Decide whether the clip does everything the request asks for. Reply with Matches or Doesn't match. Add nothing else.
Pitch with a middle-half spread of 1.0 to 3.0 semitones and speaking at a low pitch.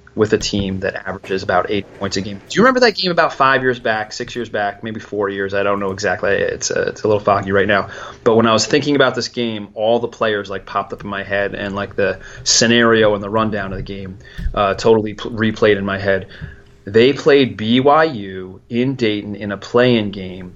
Doesn't match